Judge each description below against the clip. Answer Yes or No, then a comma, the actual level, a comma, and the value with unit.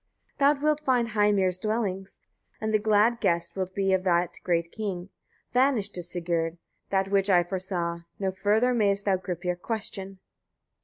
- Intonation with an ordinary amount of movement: Yes, average, 3.2 semitones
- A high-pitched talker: Yes, high, 195 Hz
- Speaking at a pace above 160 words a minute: No, average, 155 wpm